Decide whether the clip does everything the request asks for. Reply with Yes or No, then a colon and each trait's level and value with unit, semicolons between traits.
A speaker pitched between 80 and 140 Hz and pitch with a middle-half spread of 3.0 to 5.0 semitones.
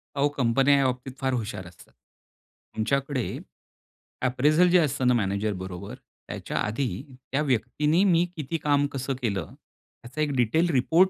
Yes: low, 135 Hz; average, 4.5 semitones